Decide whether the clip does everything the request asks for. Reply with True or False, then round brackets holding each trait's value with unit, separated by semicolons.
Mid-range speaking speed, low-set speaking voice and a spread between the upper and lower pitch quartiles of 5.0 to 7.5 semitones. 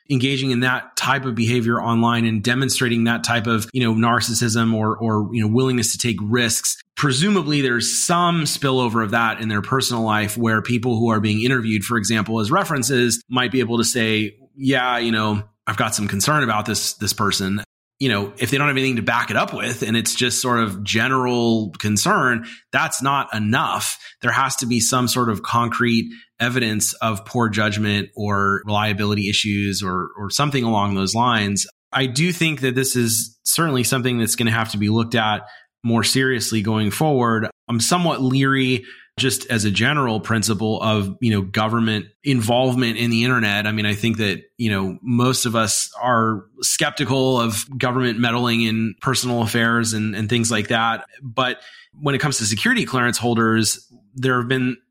False (190 wpm; 115 Hz; 2.7 semitones)